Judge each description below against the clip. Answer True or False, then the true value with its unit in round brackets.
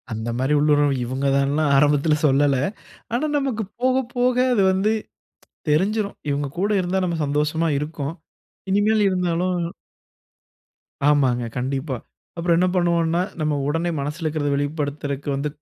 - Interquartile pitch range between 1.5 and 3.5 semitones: False (4.2 semitones)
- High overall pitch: False (155 Hz)